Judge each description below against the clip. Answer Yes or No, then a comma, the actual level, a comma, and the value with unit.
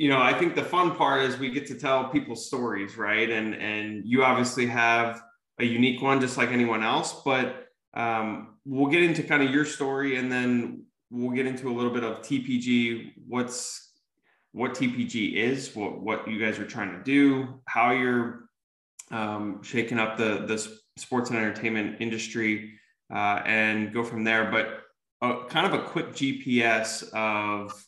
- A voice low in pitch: Yes, low, 120 Hz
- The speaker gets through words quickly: No, average, 175 wpm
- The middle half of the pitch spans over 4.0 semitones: No, average, 3.3 semitones